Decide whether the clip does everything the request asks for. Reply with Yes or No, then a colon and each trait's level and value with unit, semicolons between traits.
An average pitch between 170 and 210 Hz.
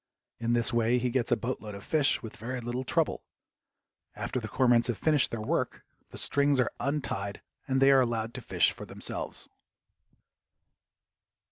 No: low, 120 Hz